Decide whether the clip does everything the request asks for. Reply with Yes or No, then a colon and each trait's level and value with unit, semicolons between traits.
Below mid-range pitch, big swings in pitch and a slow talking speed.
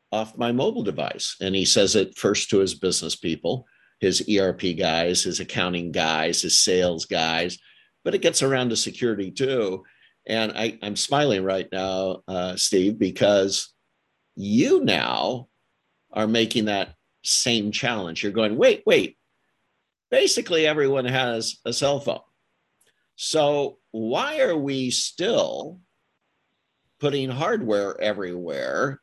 Yes: low, 110 Hz; wide, 6.1 semitones; slow, 130 wpm